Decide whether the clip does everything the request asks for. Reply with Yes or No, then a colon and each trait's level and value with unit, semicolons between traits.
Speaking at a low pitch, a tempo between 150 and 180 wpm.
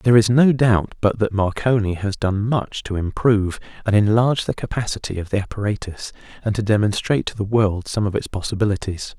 No: low, 105 Hz; average, 190 wpm